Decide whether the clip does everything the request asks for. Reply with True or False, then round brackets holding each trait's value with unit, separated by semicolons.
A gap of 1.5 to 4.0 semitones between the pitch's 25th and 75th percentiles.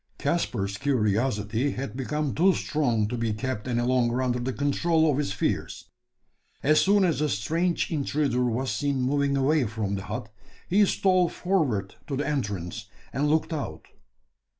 False (4.8 semitones)